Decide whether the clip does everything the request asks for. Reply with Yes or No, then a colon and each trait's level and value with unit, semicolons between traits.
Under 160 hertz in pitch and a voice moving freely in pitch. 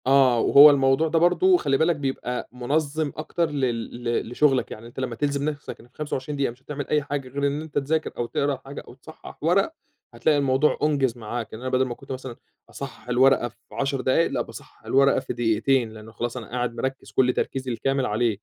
No: low, 135 Hz; average, 3.0 semitones